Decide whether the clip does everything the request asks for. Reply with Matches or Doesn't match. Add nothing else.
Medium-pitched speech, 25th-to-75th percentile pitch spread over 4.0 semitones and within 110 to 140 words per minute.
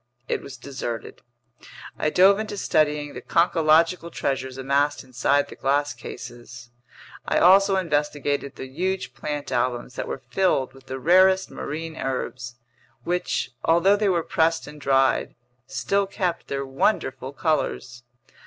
Matches